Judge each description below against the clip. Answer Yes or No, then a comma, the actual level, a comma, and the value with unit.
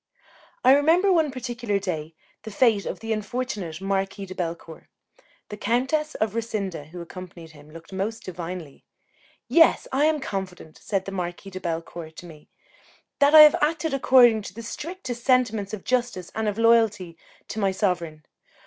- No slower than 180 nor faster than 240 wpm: No, average, 165 wpm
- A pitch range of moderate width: No, wide, 5.8 semitones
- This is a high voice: Yes, high, 205 Hz